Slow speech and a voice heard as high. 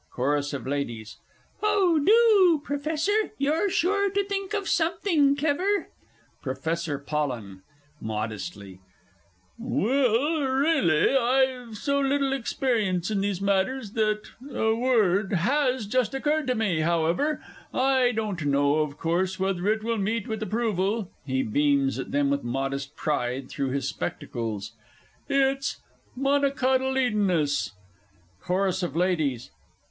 Yes: slow, 120 wpm; high, 215 Hz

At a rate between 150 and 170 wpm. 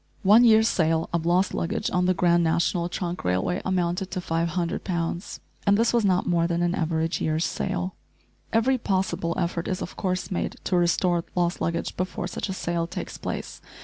No: average, 185 wpm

